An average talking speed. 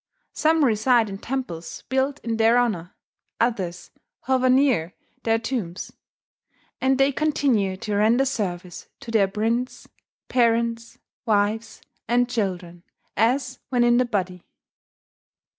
No: slow, 120 wpm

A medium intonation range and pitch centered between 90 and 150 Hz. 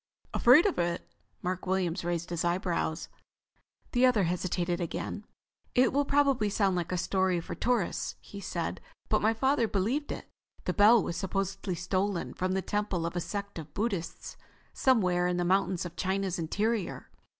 No: average, 3.5 semitones; high, 190 Hz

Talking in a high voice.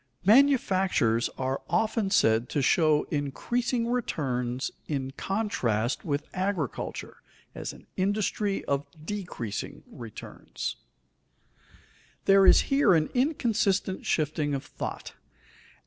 No: medium, 175 Hz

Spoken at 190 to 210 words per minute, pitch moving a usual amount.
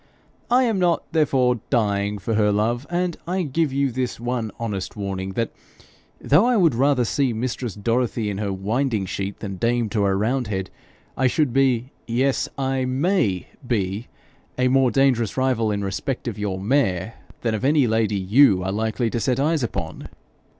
No: average, 175 wpm; average, 4.5 semitones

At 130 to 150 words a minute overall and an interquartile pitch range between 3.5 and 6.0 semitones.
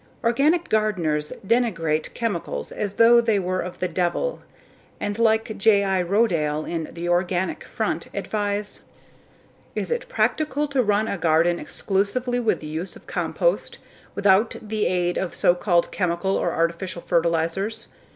Yes: average, 140 wpm; average, 4.4 semitones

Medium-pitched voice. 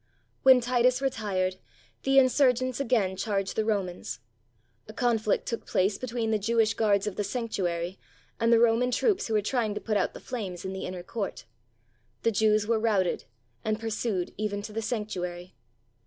No: high, 215 Hz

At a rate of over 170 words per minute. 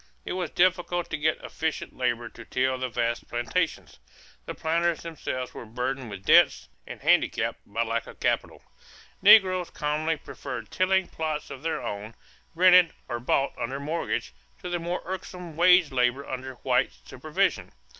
No: average, 155 wpm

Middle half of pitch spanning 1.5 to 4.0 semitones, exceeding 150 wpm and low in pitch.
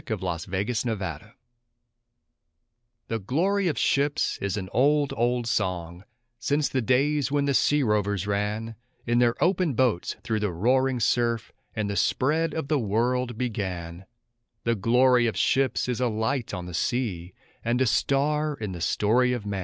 No: average, 4.6 semitones; average, 165 wpm; low, 120 Hz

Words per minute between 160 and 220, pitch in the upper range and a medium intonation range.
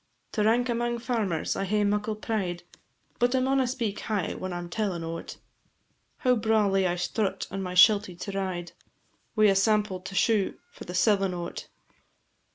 Yes: average, 170 wpm; high, 205 Hz; average, 3.5 semitones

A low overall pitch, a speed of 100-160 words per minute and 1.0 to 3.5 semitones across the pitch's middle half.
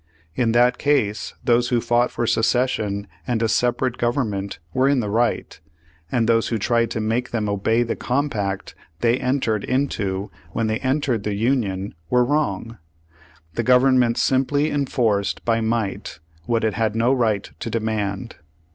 Yes: low, 115 Hz; average, 155 wpm; average, 2.8 semitones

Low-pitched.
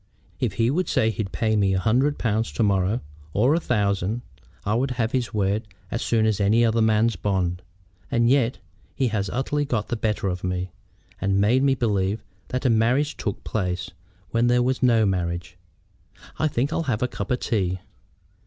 Yes: low, 110 Hz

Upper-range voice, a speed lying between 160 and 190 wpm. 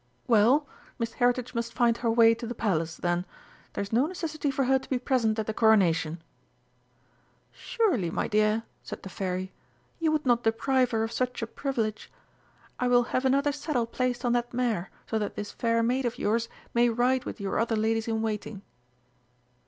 Yes: high, 230 Hz; average, 185 wpm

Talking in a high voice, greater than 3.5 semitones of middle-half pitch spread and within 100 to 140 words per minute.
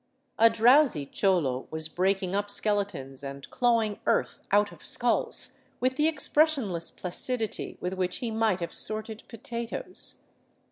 Yes: high, 205 Hz; average, 4.6 semitones; slow, 135 wpm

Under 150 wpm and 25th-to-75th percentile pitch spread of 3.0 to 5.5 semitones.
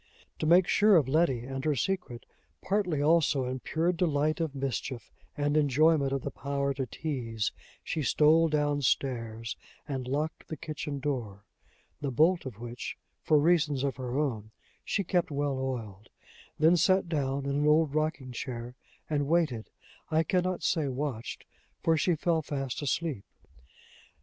No: average, 160 wpm; average, 3.4 semitones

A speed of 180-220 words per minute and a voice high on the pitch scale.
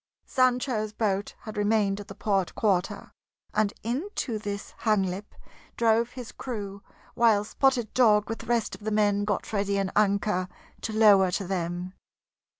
No: average, 150 wpm; high, 210 Hz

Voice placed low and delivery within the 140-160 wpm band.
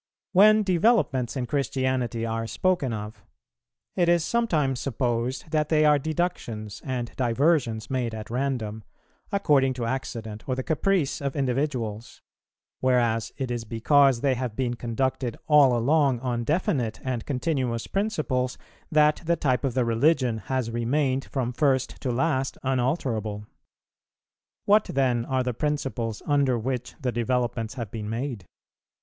Yes: low, 130 Hz; average, 145 wpm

